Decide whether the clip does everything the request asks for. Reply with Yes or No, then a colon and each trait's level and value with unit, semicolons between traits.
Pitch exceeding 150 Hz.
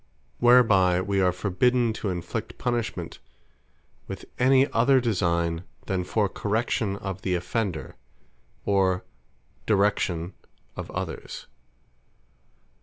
No: low, 100 Hz